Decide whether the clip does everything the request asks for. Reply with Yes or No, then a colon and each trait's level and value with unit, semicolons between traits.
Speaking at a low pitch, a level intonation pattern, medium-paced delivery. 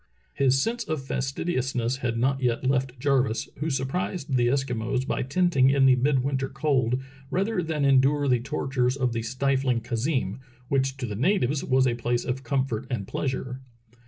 Yes: low, 130 Hz; narrow, 1.9 semitones; average, 165 wpm